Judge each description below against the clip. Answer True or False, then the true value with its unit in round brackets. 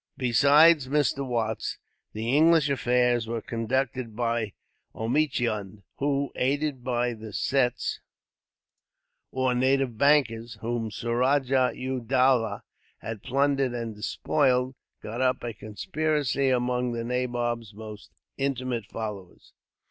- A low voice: True (125 Hz)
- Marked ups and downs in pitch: False (2.9 semitones)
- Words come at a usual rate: False (110 wpm)